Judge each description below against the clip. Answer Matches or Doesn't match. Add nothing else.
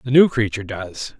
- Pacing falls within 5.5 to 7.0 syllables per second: Matches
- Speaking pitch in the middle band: Doesn't match